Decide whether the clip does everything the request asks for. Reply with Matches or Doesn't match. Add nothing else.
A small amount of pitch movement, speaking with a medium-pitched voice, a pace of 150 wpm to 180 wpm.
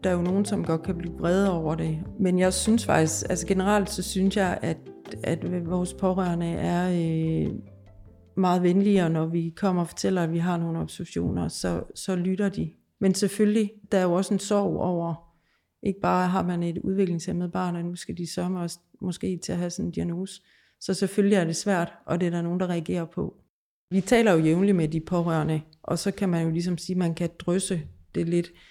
Doesn't match